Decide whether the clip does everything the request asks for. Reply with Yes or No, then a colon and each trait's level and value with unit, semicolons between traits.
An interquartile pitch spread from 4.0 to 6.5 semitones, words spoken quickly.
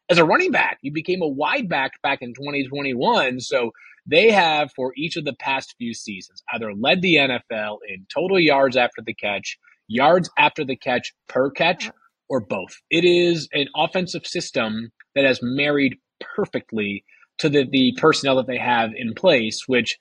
No: average, 4.3 semitones; average, 175 wpm